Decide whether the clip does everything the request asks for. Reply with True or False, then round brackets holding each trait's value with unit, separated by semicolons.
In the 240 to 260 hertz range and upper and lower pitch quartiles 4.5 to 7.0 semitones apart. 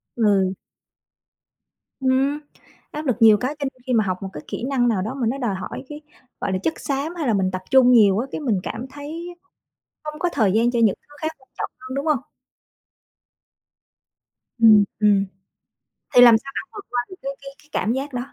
True (250 Hz; 4.8 semitones)